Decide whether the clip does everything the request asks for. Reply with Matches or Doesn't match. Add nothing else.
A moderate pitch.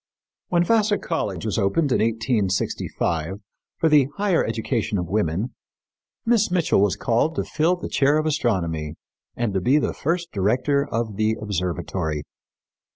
Doesn't match